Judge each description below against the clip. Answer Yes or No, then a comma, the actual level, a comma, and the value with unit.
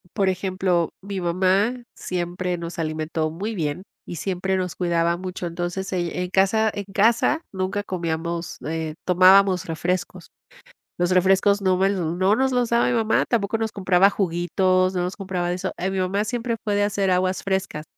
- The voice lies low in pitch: No, medium, 185 Hz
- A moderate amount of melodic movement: No, narrow, 2.2 semitones